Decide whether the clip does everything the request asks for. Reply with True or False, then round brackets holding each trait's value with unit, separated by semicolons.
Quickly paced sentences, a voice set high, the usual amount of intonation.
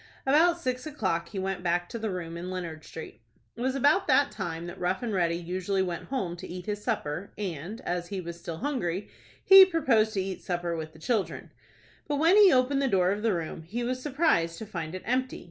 False (225 wpm; 195 Hz; 6.7 semitones)